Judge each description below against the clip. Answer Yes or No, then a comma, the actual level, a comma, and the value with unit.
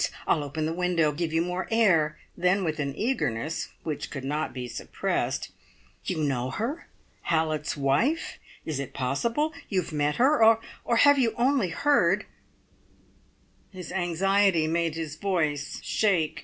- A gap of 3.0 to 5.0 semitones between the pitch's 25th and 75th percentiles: No, wide, 5.4 semitones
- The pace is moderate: Yes, average, 150 wpm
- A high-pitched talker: No, medium, 165 Hz